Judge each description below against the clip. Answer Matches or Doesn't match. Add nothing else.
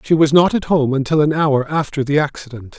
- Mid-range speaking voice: Matches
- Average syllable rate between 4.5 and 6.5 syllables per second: Matches